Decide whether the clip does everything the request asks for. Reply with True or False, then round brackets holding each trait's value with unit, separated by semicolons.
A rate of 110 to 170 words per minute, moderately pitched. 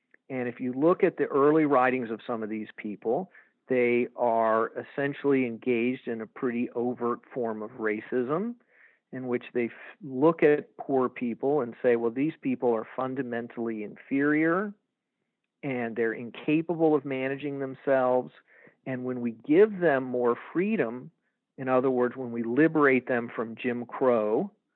False (155 wpm; 125 Hz)